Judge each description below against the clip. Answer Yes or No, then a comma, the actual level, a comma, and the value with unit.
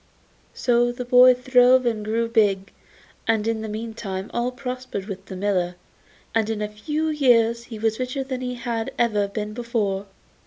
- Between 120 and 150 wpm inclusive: No, average, 170 wpm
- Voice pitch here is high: Yes, high, 230 Hz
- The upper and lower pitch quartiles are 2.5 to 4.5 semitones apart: Yes, average, 2.9 semitones